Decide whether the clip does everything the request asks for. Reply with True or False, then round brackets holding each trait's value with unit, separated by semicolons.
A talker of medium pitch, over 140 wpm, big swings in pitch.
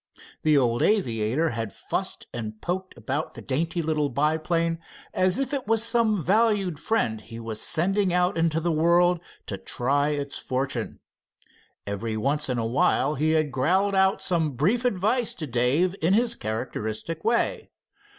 True (155 Hz; 160 wpm; 6.6 semitones)